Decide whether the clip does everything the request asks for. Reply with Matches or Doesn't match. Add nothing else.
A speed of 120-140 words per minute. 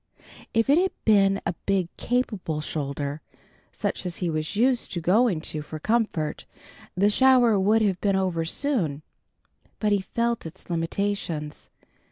Doesn't match